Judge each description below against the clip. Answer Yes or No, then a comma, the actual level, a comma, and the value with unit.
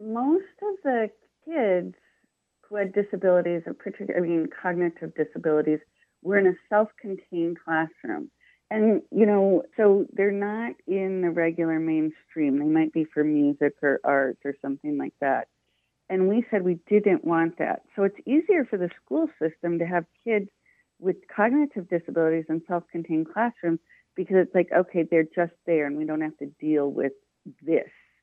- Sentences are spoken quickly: No, average, 165 wpm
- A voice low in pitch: No, medium, 175 Hz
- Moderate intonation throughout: Yes, average, 4.5 semitones